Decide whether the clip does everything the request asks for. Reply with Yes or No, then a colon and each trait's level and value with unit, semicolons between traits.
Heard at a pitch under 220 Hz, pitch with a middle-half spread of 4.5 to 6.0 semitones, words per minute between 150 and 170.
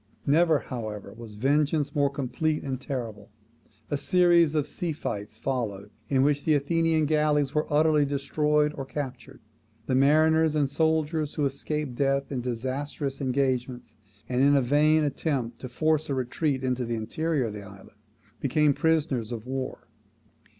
No: medium, 140 Hz; average, 3.2 semitones; average, 155 wpm